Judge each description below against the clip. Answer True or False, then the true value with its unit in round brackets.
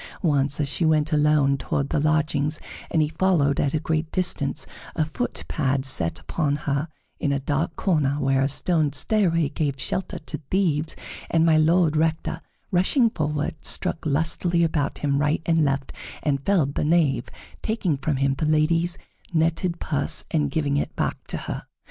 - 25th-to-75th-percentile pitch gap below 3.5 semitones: True (2.6 semitones)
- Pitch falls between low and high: True (155 Hz)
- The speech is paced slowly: False (175 wpm)